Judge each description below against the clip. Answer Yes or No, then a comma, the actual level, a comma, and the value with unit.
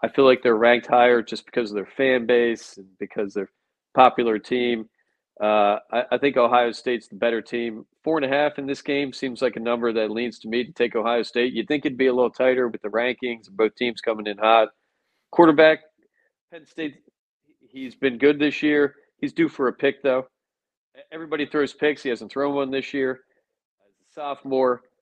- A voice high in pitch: No, low, 125 Hz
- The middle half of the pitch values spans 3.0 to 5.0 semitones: Yes, average, 3.3 semitones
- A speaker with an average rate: No, fast, 210 wpm